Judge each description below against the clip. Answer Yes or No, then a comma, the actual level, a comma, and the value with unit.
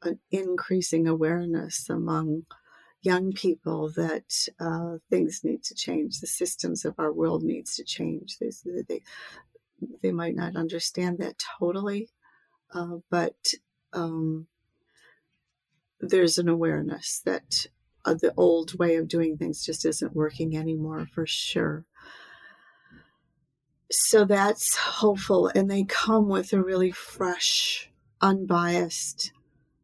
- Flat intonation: Yes, narrow, 2.3 semitones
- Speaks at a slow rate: Yes, slow, 120 wpm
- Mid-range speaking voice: Yes, medium, 170 Hz